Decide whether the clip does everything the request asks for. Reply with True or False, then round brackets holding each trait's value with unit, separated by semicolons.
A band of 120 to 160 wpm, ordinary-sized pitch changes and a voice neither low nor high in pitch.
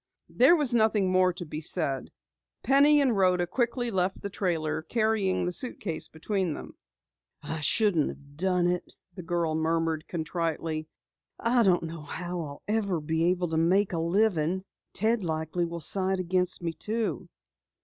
True (155 wpm; 4.0 semitones; 180 Hz)